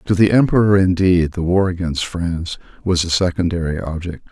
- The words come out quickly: No, average, 165 wpm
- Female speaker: No, male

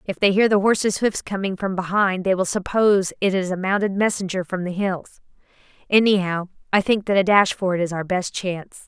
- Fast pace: Yes, fast, 215 wpm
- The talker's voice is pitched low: No, high, 190 Hz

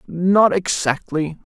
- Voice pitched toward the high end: No, medium, 175 Hz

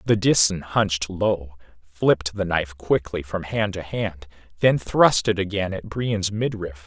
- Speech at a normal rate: Yes, average, 165 wpm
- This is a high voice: No, very low, 95 Hz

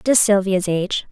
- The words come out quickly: No, average, 160 wpm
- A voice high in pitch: Yes, high, 200 Hz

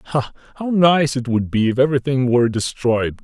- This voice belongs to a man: Yes, male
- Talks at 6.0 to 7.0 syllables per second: No, 5.4 syllables/s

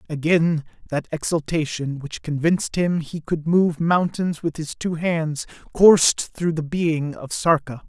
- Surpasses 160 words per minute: No, average, 150 wpm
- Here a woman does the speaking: No, male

